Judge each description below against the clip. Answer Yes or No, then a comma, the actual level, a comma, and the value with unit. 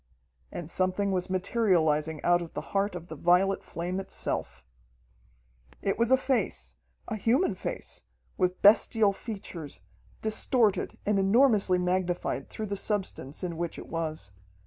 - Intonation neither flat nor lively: Yes, average, 3.5 semitones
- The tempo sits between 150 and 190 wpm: No, average, 140 wpm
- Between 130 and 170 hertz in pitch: No, medium, 185 Hz